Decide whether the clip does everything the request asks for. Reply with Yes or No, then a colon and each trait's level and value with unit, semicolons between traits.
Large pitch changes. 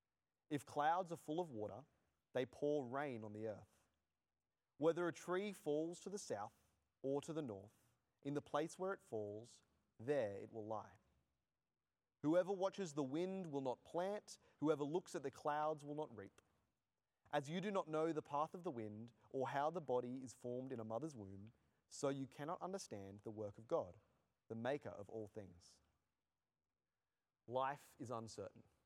Yes: wide, 6.6 semitones